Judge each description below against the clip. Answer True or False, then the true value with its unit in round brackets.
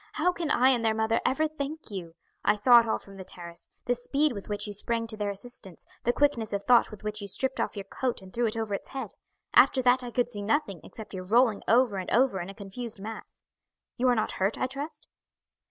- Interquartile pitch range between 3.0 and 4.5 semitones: True (3.9 semitones)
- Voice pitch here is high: True (225 Hz)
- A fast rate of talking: True (245 wpm)